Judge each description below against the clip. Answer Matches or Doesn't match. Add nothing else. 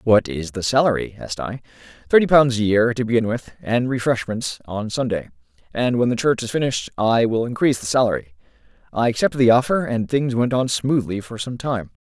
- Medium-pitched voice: Doesn't match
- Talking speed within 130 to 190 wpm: Doesn't match